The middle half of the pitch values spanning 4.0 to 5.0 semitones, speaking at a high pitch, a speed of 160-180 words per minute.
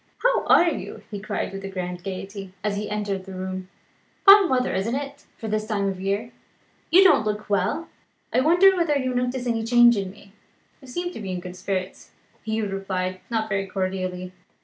No: average, 4.6 semitones; high, 210 Hz; average, 195 wpm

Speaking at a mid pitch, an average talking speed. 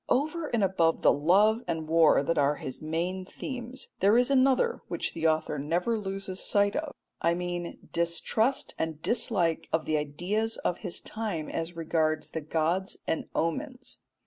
Yes: medium, 175 Hz; average, 165 wpm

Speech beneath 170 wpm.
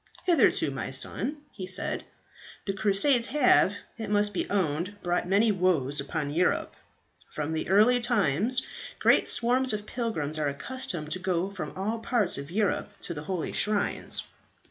Yes: average, 155 wpm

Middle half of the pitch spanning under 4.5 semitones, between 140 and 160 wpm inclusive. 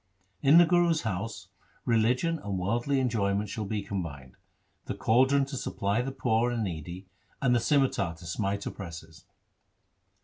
No: wide, 5.4 semitones; average, 150 wpm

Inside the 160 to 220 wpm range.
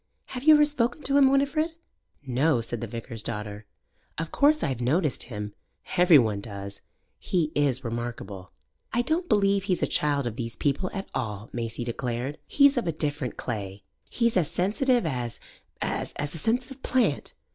Yes: average, 170 wpm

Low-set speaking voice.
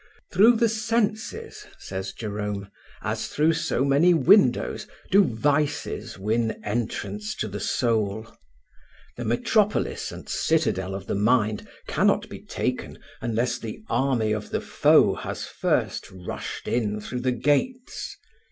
Yes: low, 120 Hz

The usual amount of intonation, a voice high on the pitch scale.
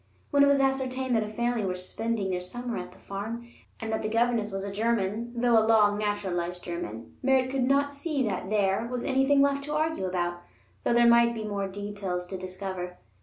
Yes: average, 4.6 semitones; high, 220 Hz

